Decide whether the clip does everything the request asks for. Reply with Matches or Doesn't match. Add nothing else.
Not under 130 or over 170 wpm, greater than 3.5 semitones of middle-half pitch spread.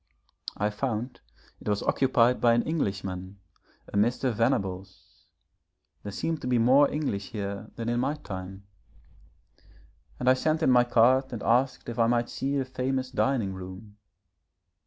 Matches